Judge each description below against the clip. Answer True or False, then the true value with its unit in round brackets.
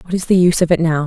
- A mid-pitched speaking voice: True (170 Hz)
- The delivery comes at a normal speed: False (395 wpm)